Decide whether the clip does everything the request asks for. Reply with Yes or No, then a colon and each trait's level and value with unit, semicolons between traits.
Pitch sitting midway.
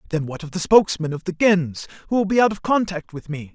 Yes: medium, 175 Hz